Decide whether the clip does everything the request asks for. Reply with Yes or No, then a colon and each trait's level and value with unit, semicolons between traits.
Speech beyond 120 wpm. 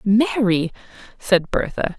No: slow, 90 wpm